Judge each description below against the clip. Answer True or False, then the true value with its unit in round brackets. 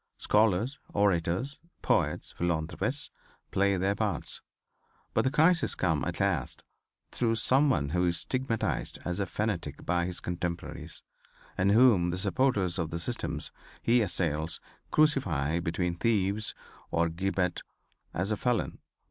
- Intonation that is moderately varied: True (4.9 semitones)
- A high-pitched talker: False (95 Hz)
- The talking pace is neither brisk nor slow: False (130 wpm)